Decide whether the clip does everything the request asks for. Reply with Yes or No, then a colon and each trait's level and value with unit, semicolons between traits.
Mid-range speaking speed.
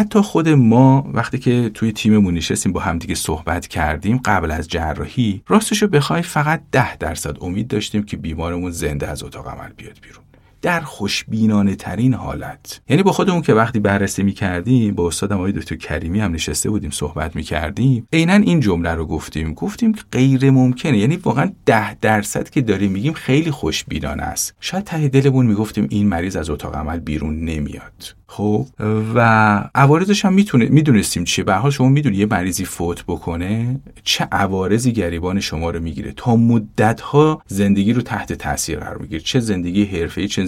No: fast, 170 wpm